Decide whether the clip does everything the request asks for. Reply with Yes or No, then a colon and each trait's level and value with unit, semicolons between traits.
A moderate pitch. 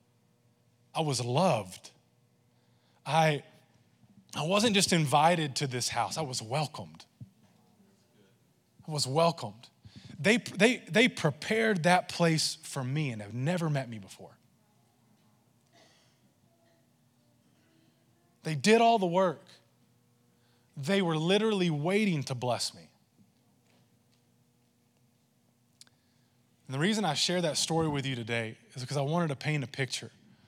Yes: medium, 150 Hz